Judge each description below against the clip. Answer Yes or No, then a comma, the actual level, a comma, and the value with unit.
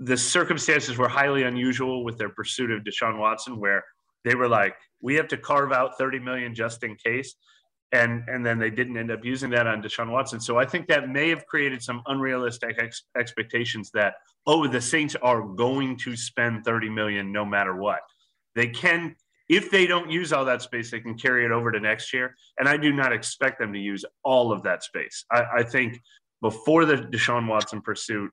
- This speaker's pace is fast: Yes, fast, 210 wpm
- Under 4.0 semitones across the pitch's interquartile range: Yes, average, 2.7 semitones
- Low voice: Yes, low, 120 Hz